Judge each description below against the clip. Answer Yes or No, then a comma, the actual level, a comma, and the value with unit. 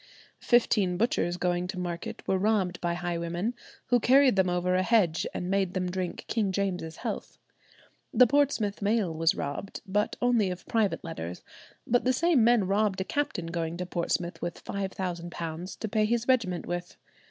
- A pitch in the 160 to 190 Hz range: Yes, medium, 185 Hz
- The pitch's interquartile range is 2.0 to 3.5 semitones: No, average, 3.9 semitones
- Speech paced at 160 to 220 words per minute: Yes, average, 170 wpm